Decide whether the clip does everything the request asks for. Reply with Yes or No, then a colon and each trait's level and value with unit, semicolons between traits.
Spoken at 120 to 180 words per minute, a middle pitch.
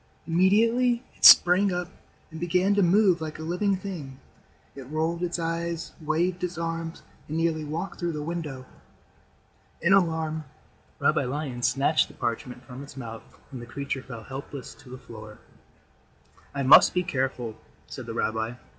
Yes: average, 160 wpm; medium, 160 Hz